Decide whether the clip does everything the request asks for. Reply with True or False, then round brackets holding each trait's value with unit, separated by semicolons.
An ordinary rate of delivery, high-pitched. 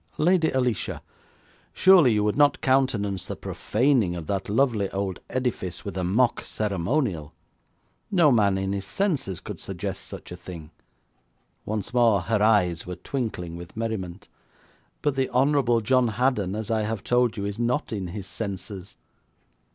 False (155 wpm; 110 Hz)